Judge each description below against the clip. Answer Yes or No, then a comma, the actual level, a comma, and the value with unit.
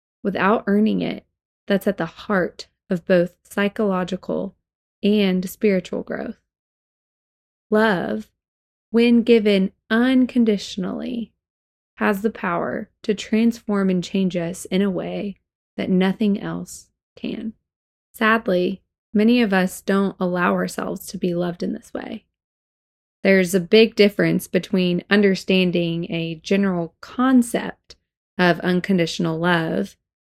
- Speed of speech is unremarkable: No, slow, 115 wpm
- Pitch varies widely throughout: No, average, 3.3 semitones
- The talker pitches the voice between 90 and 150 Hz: No, high, 195 Hz